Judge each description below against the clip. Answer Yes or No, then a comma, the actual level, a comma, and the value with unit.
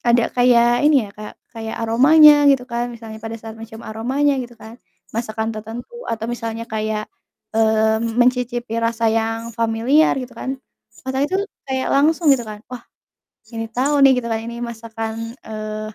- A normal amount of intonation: No, narrow, 2.1 semitones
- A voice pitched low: No, high, 230 Hz